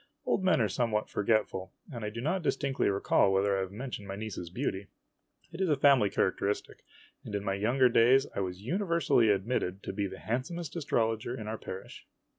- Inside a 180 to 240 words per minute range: Yes, average, 195 wpm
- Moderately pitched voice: No, low, 110 Hz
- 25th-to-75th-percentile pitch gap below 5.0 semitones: No, average, 5.3 semitones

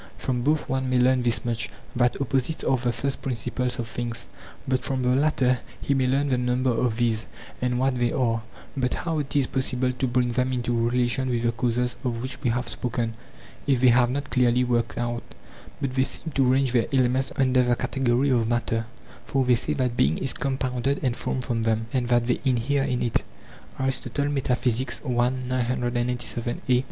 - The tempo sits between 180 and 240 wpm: Yes, average, 185 wpm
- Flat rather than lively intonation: Yes, narrow, 1.6 semitones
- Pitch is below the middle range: Yes, low, 125 Hz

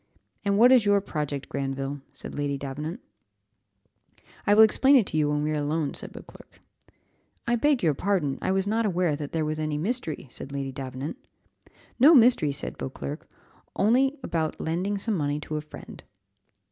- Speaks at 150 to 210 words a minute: Yes, average, 175 wpm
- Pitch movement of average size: No, wide, 6.3 semitones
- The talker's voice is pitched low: No, medium, 155 Hz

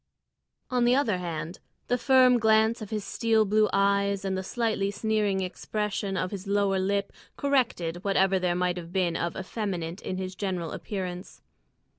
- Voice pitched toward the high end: Yes, high, 195 Hz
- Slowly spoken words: No, average, 160 wpm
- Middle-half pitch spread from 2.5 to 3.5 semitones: Yes, average, 2.8 semitones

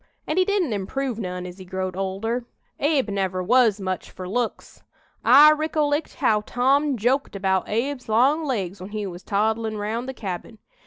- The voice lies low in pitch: No, high, 220 Hz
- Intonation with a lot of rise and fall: Yes, wide, 5.9 semitones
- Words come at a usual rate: Yes, average, 170 wpm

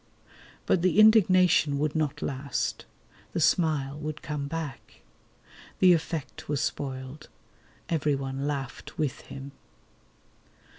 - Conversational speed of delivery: No, slow, 105 wpm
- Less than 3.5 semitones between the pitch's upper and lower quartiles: Yes, average, 2.9 semitones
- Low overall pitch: No, medium, 150 Hz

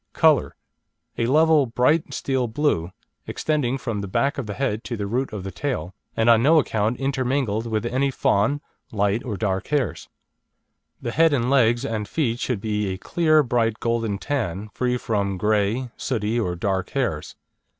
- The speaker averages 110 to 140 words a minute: No, average, 170 wpm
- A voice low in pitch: Yes, low, 115 Hz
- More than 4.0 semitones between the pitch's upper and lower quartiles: Yes, average, 4.4 semitones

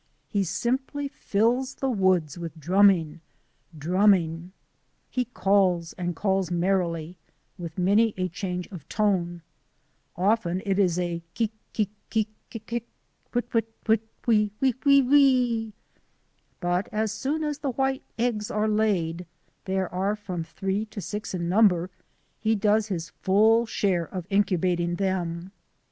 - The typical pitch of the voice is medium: No, high, 195 Hz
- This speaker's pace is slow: No, average, 150 wpm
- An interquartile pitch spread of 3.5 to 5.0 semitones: Yes, average, 4.0 semitones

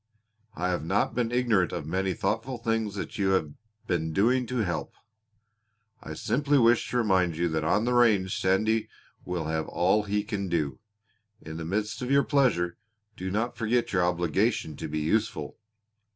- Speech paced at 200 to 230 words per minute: No, average, 175 wpm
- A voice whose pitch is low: Yes, very low, 95 Hz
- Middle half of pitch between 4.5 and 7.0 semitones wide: Yes, average, 4.8 semitones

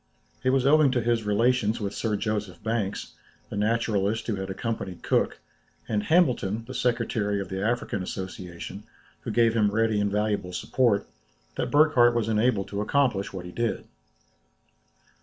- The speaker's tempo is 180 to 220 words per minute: No, average, 160 wpm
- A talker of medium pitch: No, low, 110 Hz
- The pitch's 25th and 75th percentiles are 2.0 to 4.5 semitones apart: Yes, average, 2.9 semitones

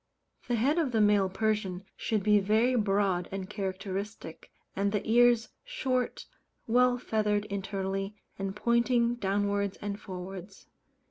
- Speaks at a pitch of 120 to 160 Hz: No, high, 205 Hz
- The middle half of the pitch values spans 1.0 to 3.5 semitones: Yes, average, 3.1 semitones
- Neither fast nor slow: No, slow, 130 wpm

